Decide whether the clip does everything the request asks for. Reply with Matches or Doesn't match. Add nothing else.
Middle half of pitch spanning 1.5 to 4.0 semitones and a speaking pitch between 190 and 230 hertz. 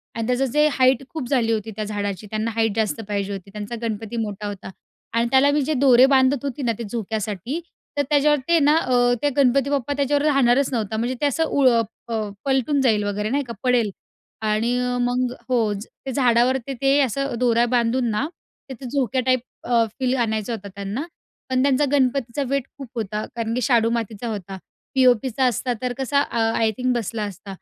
Doesn't match